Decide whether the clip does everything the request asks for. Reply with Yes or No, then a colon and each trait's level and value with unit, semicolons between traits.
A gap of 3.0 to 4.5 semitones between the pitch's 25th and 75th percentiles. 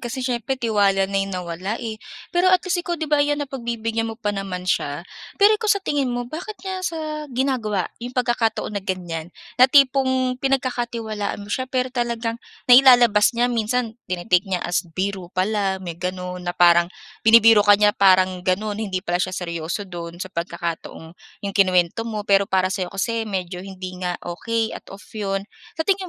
No: average, 5.2 semitones